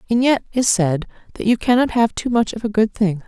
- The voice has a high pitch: Yes, high, 220 Hz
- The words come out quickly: Yes, fast, 255 wpm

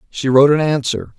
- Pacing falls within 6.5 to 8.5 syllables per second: No, 6.1 syllables/s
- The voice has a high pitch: No, medium, 140 Hz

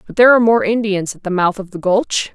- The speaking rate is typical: No, fast, 280 wpm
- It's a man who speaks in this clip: No, female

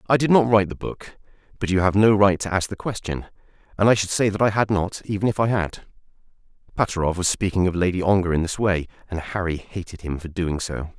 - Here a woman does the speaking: No, male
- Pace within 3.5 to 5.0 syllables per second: No, 6.1 syllables/s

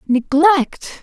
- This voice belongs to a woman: Yes, female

